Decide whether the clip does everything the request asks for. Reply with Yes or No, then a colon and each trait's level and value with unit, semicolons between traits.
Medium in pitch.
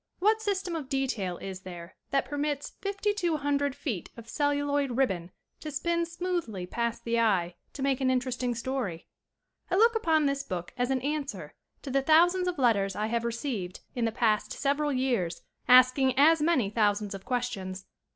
No: very high, 265 Hz